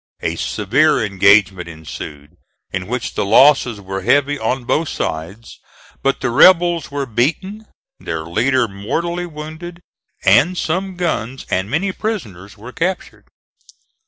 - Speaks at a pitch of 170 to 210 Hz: No, low, 130 Hz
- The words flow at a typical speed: No, slow, 130 wpm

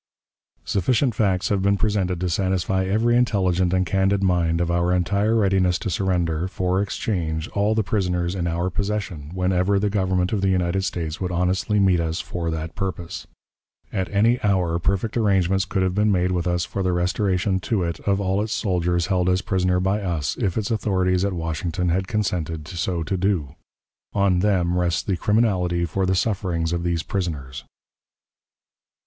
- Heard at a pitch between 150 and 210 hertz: No, very low, 95 Hz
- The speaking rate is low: No, average, 180 wpm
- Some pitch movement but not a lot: No, narrow, 2.2 semitones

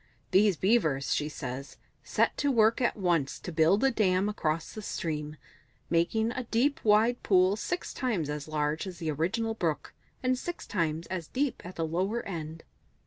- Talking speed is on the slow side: No, average, 175 wpm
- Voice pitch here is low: No, medium, 185 Hz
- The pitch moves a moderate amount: No, wide, 6.1 semitones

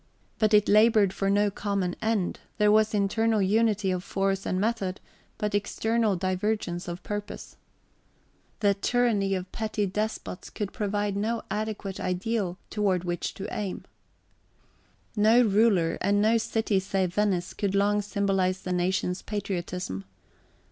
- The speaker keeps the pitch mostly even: Yes, narrow, 2.3 semitones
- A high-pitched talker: Yes, high, 200 Hz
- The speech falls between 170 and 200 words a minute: No, average, 140 wpm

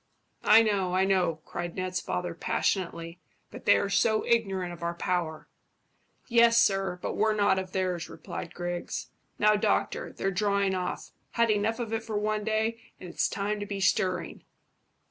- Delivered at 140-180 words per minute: Yes, average, 170 wpm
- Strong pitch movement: No, average, 3.1 semitones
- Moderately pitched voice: No, high, 195 Hz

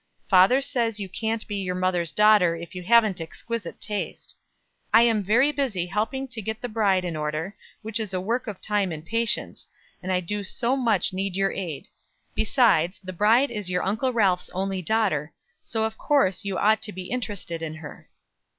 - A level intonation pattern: No, average, 3.7 semitones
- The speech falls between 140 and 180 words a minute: No, average, 190 wpm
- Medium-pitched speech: No, high, 205 Hz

